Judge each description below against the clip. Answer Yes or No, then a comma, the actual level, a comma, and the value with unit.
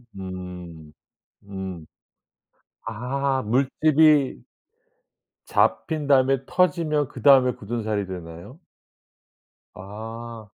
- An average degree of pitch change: No, wide, 6.4 semitones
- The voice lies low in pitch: Yes, low, 115 Hz